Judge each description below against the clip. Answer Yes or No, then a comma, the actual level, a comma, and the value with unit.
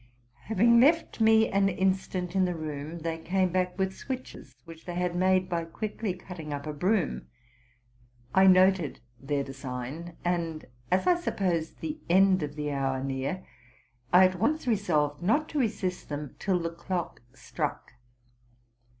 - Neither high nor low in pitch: Yes, medium, 180 Hz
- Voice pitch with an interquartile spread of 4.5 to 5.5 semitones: No, average, 3.9 semitones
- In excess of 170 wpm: No, average, 155 wpm